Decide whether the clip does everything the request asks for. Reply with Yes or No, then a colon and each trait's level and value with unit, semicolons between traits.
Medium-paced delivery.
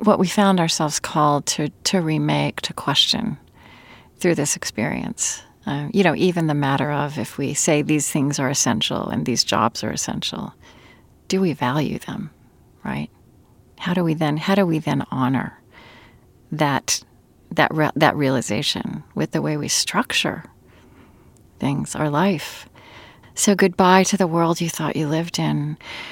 Yes: average, 160 wpm